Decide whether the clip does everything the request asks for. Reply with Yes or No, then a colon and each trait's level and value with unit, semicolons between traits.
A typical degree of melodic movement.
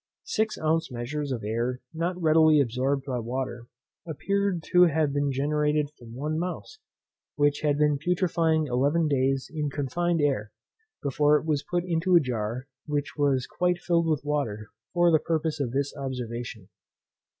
Yes: average, 3.7 semitones